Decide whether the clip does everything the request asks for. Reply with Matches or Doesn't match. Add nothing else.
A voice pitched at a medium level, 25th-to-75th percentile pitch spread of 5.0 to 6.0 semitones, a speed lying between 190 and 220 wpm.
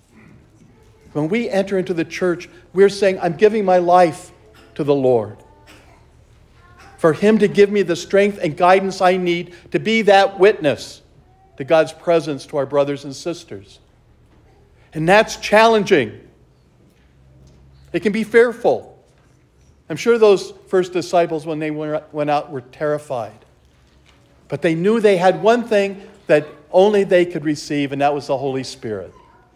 Doesn't match